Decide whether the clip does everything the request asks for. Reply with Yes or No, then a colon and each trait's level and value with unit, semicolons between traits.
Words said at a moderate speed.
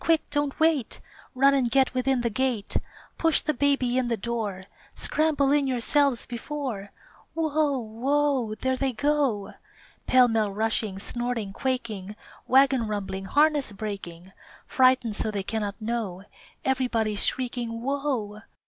No: slow, 130 wpm